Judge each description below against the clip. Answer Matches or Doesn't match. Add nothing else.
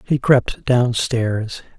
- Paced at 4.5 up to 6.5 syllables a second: Doesn't match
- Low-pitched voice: Matches